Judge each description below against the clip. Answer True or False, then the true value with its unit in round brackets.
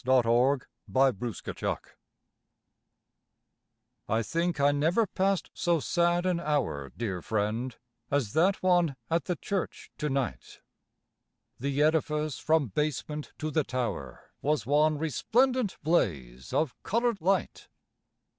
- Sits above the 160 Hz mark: False (150 Hz)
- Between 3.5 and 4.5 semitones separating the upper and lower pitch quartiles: False (5.6 semitones)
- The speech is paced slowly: True (115 wpm)